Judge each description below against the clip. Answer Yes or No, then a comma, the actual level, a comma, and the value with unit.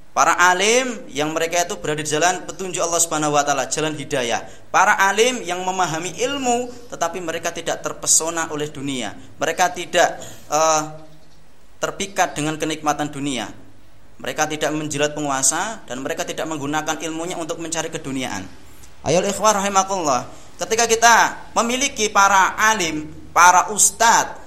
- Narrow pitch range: No, average, 3.9 semitones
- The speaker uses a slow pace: No, average, 135 wpm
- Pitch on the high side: No, medium, 160 Hz